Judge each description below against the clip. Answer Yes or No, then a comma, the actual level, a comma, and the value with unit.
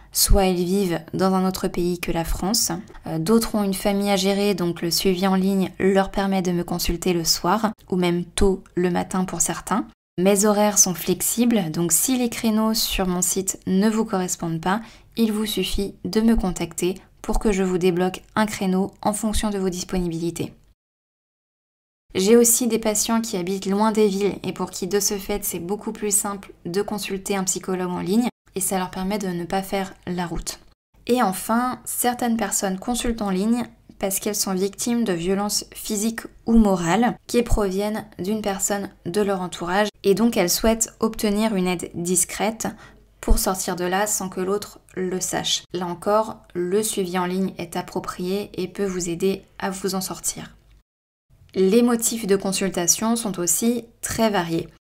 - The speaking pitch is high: Yes, high, 195 Hz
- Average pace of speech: Yes, average, 185 wpm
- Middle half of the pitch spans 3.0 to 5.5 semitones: No, narrow, 2.6 semitones